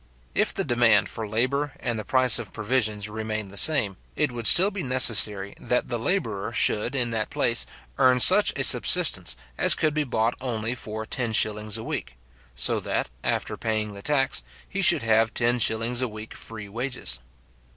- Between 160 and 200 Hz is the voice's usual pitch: No, low, 115 Hz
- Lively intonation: No, average, 2.8 semitones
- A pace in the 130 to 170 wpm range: No, average, 180 wpm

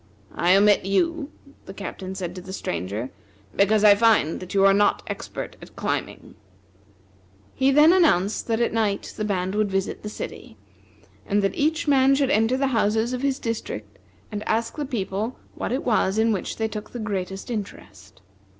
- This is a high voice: Yes, high, 210 Hz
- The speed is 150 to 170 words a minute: No, average, 180 wpm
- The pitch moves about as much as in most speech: Yes, average, 4.0 semitones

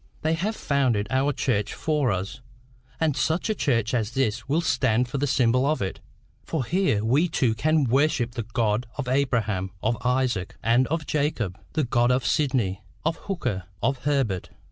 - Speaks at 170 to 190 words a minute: Yes, average, 175 wpm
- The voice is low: Yes, low, 125 Hz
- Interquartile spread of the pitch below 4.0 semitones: No, average, 4.5 semitones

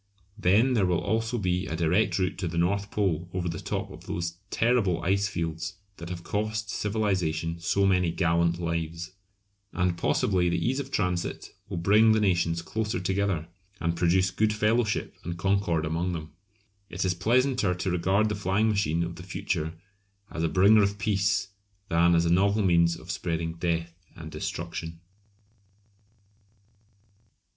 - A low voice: Yes, very low, 90 Hz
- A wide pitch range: No, average, 3.2 semitones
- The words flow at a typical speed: Yes, average, 160 wpm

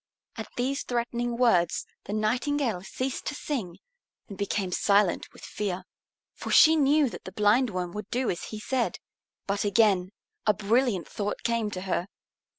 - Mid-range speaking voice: No, high, 215 Hz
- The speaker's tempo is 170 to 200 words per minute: No, average, 155 wpm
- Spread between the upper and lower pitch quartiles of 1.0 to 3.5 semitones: No, average, 4.3 semitones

